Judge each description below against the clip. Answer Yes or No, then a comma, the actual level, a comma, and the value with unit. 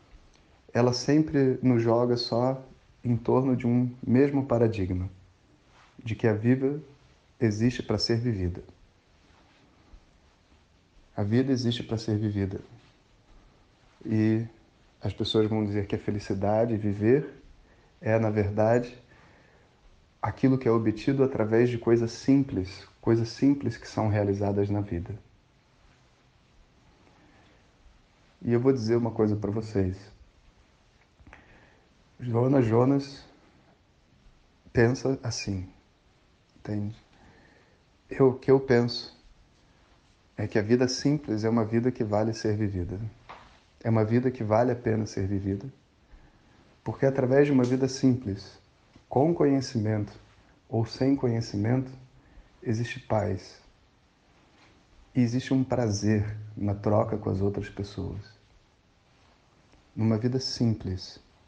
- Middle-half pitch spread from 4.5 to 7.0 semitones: No, average, 3.7 semitones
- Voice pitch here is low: Yes, low, 110 Hz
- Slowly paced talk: Yes, slow, 115 wpm